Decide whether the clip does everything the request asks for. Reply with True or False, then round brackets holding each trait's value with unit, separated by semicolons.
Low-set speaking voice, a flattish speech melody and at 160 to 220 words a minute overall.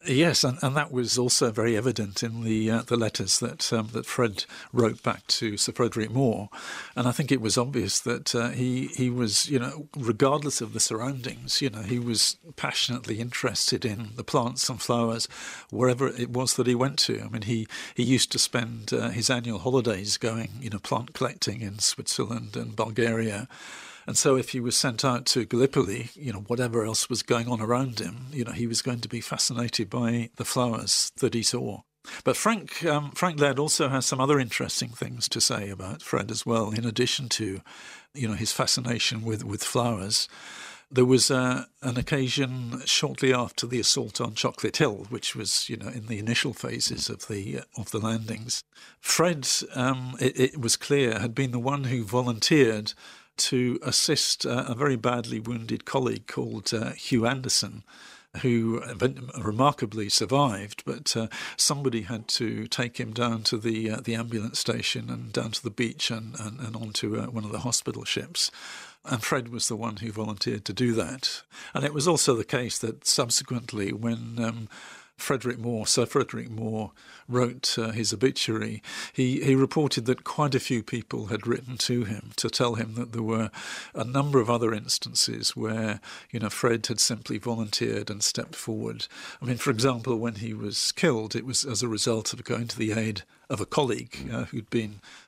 True (120 Hz; 2.3 semitones; 190 wpm)